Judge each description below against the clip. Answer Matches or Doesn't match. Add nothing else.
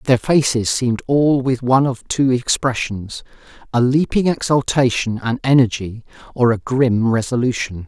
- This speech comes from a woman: Doesn't match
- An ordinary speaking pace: Doesn't match